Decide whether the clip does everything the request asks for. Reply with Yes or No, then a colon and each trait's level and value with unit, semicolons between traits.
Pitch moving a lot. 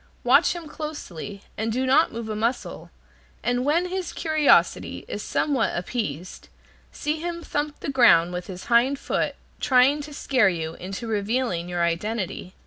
Yes: wide, 7.6 semitones